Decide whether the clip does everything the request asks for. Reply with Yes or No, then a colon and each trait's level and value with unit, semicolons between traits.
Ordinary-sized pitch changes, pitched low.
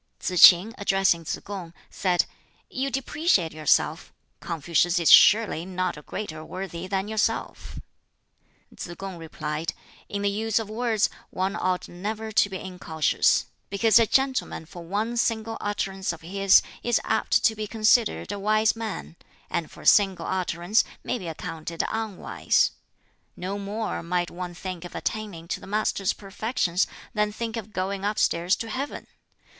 No: average, 3.7 semitones; high, 195 Hz